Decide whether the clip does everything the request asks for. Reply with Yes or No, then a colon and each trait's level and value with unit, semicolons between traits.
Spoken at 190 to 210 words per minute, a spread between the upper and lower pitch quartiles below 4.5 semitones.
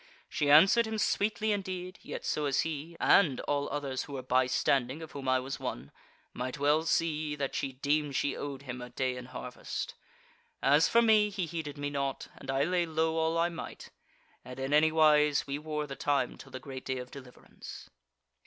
Yes: average, 200 wpm; average, 3.3 semitones